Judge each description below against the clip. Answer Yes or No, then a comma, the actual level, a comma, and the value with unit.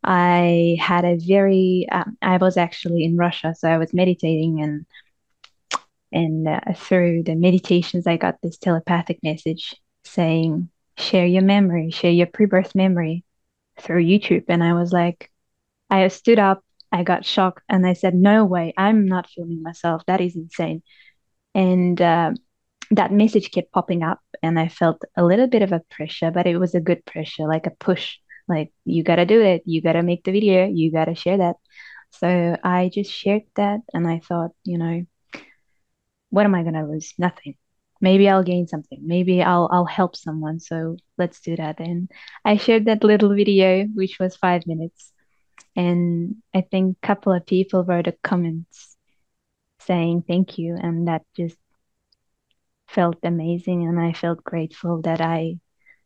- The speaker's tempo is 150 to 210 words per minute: Yes, average, 170 wpm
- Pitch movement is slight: Yes, narrow, 2.0 semitones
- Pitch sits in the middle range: Yes, medium, 175 Hz